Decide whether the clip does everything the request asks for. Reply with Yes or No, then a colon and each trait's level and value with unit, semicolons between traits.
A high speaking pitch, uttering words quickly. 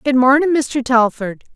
No: very high, 260 Hz; average, 155 wpm